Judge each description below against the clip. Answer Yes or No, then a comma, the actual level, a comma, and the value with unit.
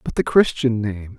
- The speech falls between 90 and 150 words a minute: No, average, 200 wpm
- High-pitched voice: No, low, 115 Hz